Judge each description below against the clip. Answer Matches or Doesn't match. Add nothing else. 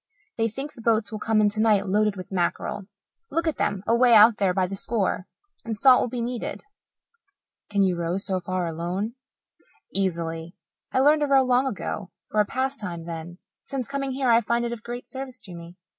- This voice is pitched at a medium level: Doesn't match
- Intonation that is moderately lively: Matches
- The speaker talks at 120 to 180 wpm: Doesn't match